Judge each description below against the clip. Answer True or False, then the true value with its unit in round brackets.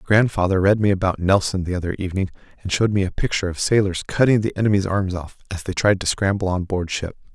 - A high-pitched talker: False (95 Hz)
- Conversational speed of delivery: False (230 wpm)